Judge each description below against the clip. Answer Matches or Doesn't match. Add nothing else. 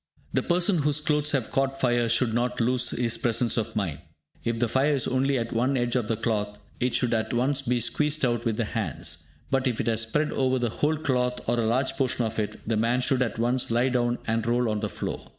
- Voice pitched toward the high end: Doesn't match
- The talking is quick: Matches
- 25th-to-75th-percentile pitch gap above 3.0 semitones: Doesn't match